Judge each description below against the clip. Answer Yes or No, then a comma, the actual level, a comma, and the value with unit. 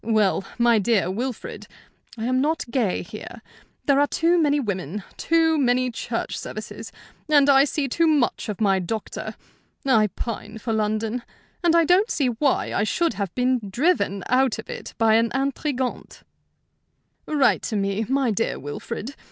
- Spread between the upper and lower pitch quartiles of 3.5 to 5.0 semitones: Yes, average, 4.7 semitones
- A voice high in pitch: Yes, high, 245 Hz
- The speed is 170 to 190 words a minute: No, average, 160 wpm